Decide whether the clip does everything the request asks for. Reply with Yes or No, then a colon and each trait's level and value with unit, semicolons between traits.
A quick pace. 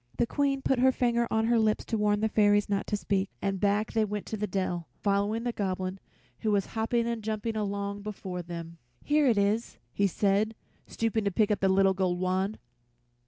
Yes: fast, 210 wpm